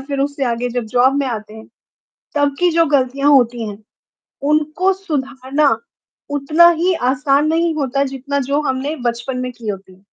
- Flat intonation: No, average, 3.1 semitones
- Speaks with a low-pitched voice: No, very high, 275 Hz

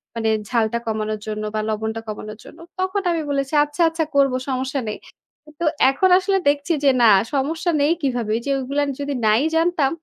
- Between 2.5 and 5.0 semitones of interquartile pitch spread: No, wide, 5.4 semitones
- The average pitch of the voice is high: Yes, very high, 275 Hz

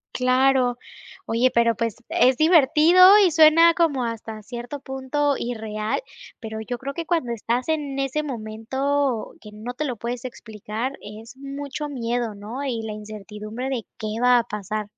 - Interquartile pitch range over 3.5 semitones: Yes, average, 4.1 semitones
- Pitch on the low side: No, high, 245 Hz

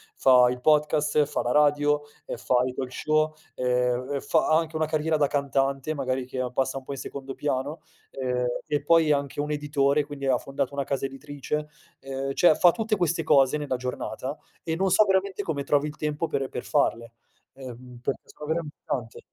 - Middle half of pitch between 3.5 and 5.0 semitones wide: No, narrow, 2.6 semitones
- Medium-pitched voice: Yes, medium, 145 Hz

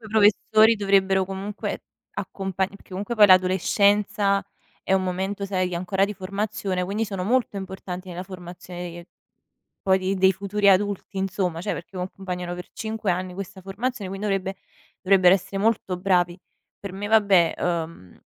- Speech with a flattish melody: Yes, narrow, 1.7 semitones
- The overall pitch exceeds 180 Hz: Yes, high, 190 Hz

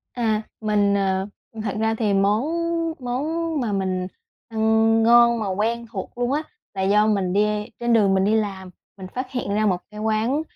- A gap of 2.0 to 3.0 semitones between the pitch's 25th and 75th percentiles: Yes, narrow, 2.6 semitones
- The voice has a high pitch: Yes, high, 215 Hz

